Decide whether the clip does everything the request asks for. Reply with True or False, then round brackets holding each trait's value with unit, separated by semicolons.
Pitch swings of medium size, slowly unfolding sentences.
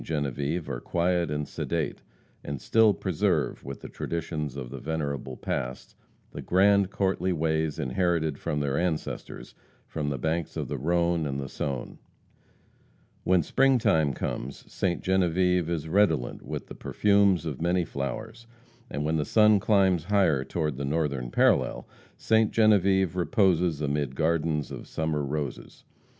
False (4.3 semitones; 145 wpm)